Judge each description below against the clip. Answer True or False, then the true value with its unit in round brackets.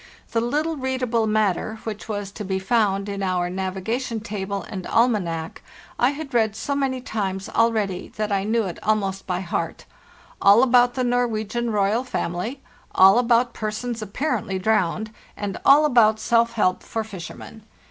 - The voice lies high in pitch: True (215 Hz)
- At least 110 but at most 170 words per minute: True (160 wpm)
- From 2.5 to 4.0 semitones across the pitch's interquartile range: True (3.6 semitones)